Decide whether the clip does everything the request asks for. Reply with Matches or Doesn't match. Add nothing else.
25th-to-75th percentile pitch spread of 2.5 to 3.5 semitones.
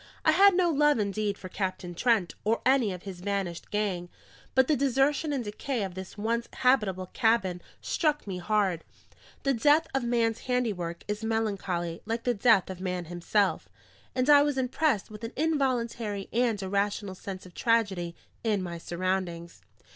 Doesn't match